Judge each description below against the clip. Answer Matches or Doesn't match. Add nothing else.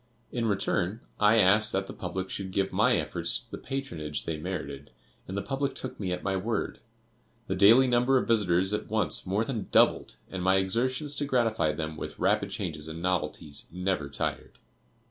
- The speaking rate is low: Doesn't match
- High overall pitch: Doesn't match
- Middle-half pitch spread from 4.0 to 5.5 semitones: Matches